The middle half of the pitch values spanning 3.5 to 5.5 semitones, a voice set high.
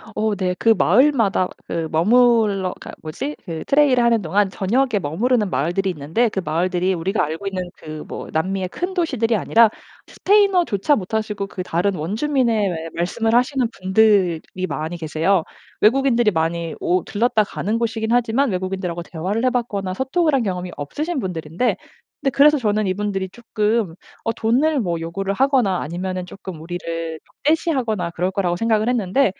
Yes: average, 5.1 semitones; high, 200 Hz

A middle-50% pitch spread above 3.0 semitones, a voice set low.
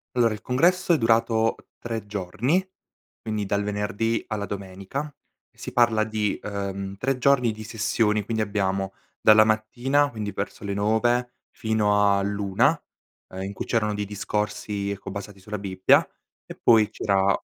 No: narrow, 2.4 semitones; low, 105 Hz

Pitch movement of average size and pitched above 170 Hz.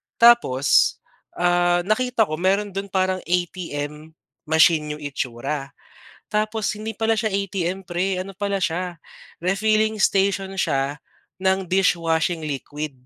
Yes: average, 3.9 semitones; medium, 185 Hz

